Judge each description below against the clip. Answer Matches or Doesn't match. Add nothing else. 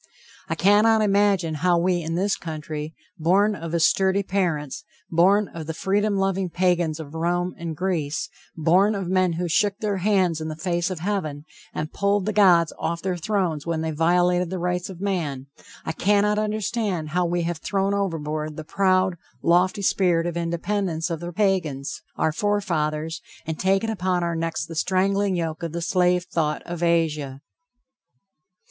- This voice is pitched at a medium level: Matches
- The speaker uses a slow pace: Doesn't match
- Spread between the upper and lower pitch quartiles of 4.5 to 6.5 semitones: Doesn't match